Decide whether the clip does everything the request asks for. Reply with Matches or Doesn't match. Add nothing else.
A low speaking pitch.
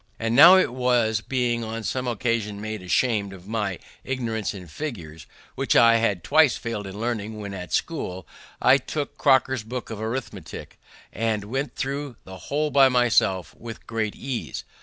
Matches